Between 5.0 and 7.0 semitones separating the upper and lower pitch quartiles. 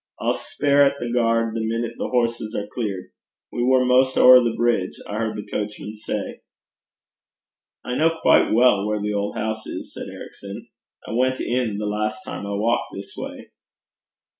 No: average, 2.8 semitones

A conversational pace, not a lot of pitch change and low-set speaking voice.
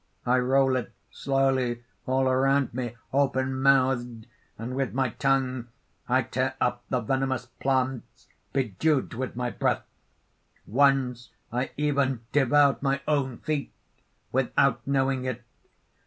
No: slow, 125 wpm; narrow, 1.8 semitones; low, 130 Hz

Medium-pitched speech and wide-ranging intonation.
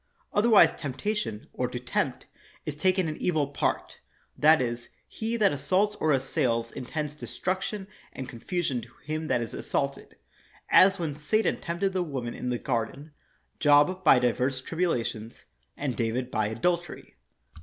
Yes: medium, 150 Hz; wide, 6.4 semitones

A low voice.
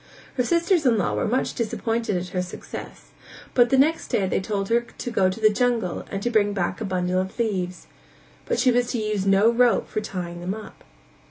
No: high, 215 Hz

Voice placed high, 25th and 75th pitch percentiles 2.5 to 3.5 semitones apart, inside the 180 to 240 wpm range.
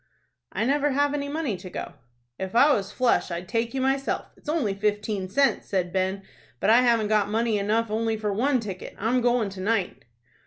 No: high, 220 Hz; average, 4.4 semitones; average, 200 wpm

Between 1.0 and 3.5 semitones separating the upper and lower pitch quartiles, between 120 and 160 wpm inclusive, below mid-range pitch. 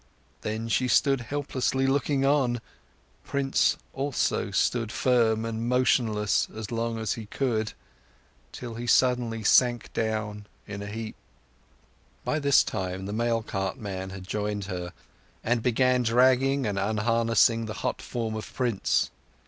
Yes: average, 2.9 semitones; average, 140 wpm; low, 115 Hz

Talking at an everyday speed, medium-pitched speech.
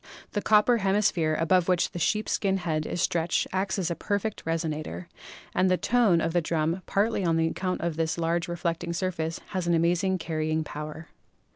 Yes: average, 175 wpm; medium, 170 Hz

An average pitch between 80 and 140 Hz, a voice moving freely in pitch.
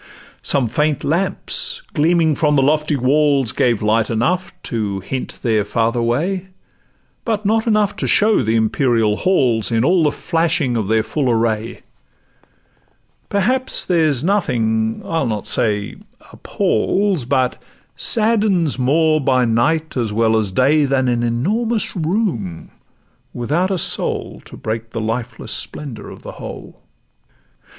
Yes: low, 135 Hz; wide, 6.9 semitones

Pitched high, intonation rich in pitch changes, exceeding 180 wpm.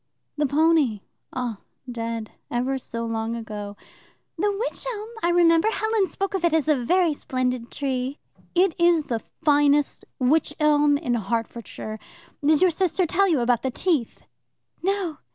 No: very high, 290 Hz; wide, 6.3 semitones; average, 150 wpm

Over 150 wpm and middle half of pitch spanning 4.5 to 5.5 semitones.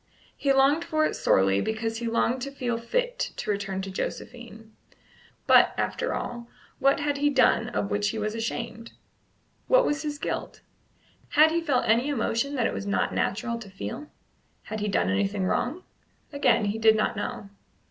Yes: average, 180 wpm; average, 4.8 semitones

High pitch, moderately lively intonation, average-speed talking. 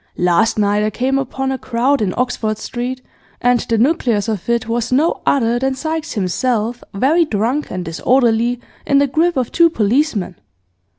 Yes: high, 245 Hz; average, 3.7 semitones; average, 170 wpm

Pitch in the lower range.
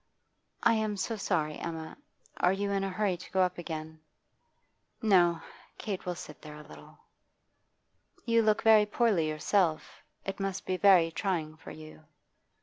No: medium, 185 Hz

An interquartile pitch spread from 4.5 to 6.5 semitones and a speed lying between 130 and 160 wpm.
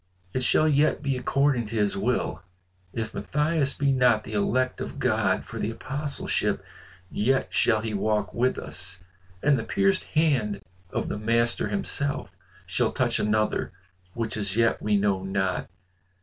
Yes: average, 4.8 semitones; average, 155 wpm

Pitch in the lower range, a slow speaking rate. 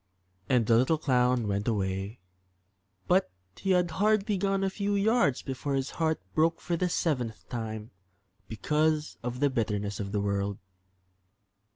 No: low, 130 Hz; average, 150 wpm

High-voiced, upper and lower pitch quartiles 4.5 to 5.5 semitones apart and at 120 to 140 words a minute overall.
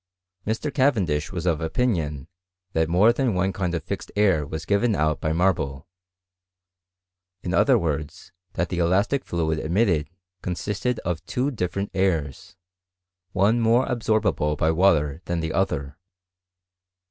No: very low, 90 Hz; average, 5.0 semitones; slow, 135 wpm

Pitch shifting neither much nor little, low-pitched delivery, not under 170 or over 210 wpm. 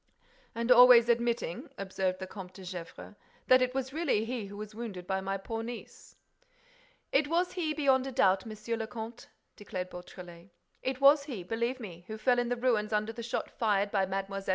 No: average, 4.4 semitones; high, 225 Hz; average, 195 wpm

